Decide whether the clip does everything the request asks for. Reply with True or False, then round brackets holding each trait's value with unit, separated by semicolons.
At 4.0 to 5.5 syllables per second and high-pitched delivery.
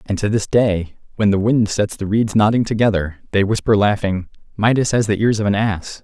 False (5.2 syllables/s; 105 Hz)